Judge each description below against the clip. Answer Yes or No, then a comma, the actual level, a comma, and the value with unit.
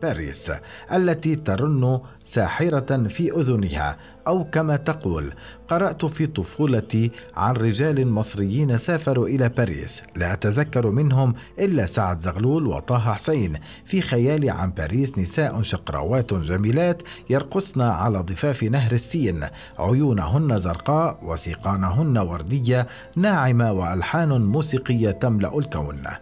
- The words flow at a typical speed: Yes, average, 110 wpm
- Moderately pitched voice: No, low, 120 Hz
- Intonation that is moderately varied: No, wide, 7.1 semitones